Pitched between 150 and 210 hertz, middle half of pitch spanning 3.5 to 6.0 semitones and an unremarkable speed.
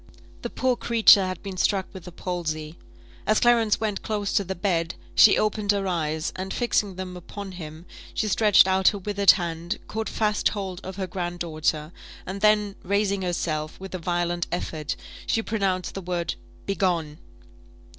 No: high, 190 Hz; average, 2.9 semitones; average, 170 wpm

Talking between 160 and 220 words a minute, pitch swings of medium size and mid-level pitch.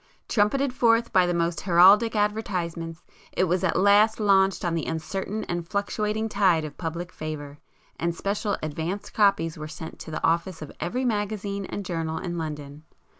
Yes: average, 170 wpm; average, 4.1 semitones; medium, 180 Hz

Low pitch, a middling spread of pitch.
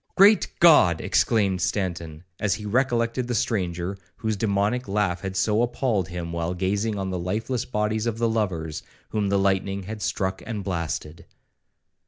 Yes: low, 100 Hz; average, 3.5 semitones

